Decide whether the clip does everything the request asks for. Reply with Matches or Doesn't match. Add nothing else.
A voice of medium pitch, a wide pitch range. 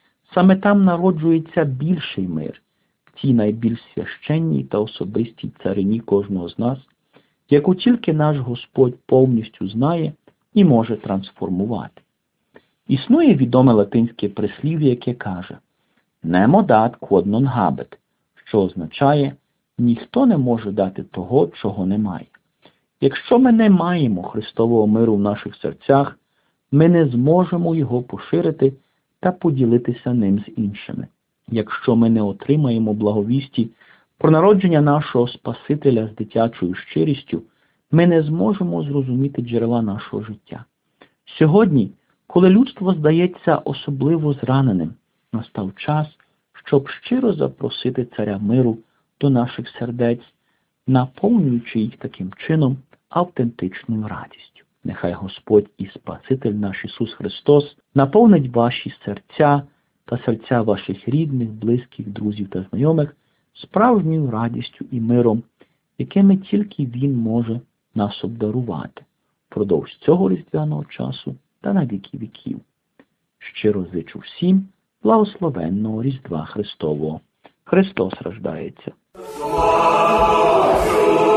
Doesn't match